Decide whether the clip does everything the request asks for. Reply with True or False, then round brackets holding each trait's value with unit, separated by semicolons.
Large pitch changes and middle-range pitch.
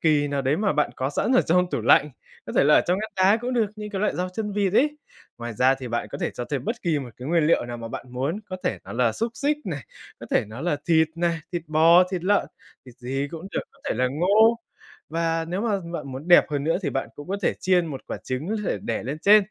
True (6.3 semitones; 165 Hz)